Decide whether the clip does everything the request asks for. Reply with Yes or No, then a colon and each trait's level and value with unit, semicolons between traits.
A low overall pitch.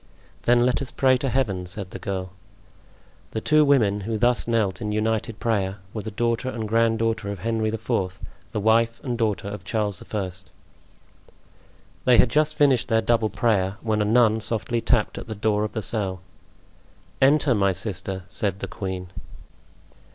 Yes: low, 110 Hz